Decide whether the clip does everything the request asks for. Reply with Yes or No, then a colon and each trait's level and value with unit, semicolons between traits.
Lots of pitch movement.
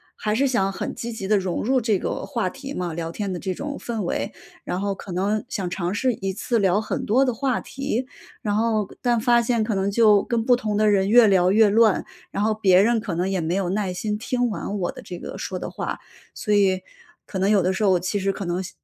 No: average, 3.4 semitones